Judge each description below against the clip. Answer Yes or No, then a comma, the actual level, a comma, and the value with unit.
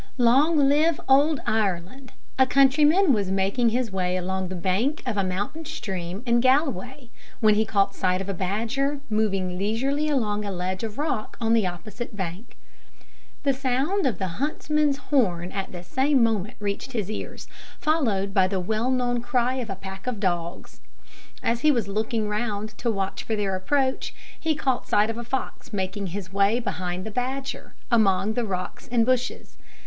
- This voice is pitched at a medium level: No, high, 220 Hz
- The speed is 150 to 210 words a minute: Yes, average, 175 wpm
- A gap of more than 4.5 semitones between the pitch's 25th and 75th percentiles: Yes, average, 5.3 semitones